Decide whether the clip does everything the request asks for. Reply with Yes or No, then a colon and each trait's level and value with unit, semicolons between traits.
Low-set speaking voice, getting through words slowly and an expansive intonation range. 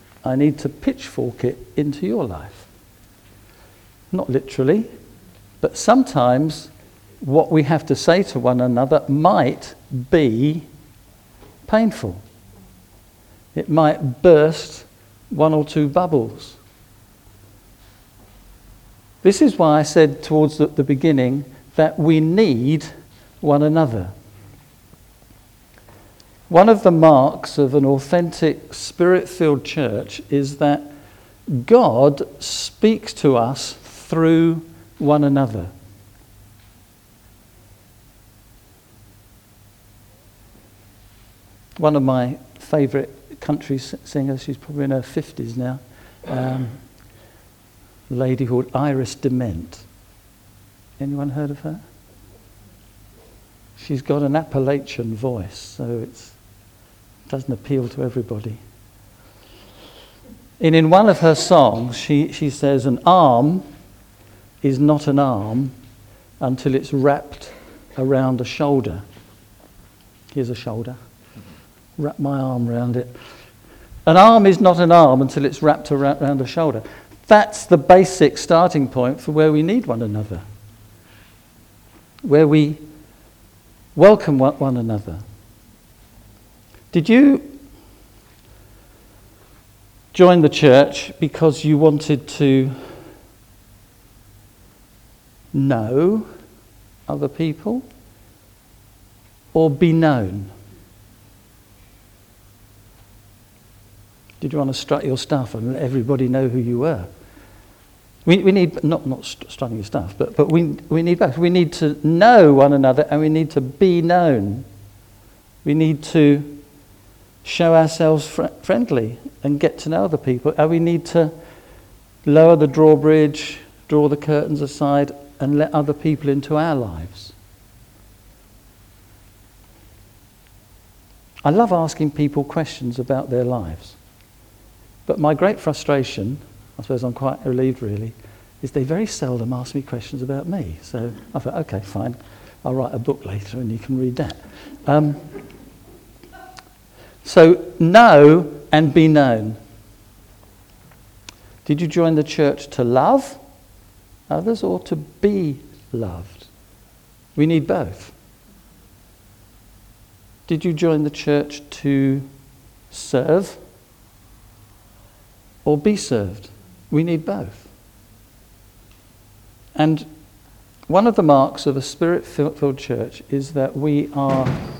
Yes: low, 125 Hz; slow, 115 wpm; wide, 6.2 semitones